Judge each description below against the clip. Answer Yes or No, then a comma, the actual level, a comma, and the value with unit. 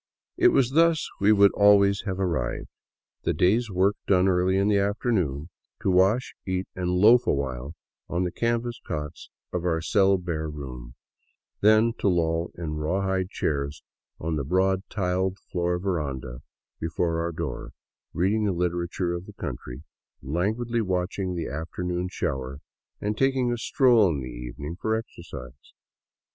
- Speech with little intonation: No, average, 4.2 semitones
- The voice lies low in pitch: Yes, very low, 90 Hz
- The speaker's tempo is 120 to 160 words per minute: Yes, average, 155 wpm